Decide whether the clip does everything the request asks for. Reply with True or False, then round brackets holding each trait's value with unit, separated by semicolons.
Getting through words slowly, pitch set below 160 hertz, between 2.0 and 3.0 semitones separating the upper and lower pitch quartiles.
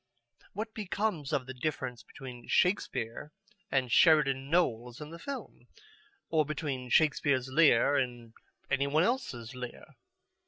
False (125 wpm; 140 Hz; 4.5 semitones)